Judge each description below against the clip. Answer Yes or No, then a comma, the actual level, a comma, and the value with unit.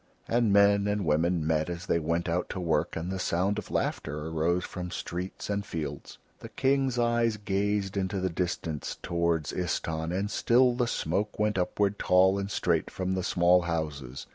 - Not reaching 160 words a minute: No, average, 180 wpm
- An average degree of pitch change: Yes, average, 3.5 semitones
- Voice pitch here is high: No, very low, 90 Hz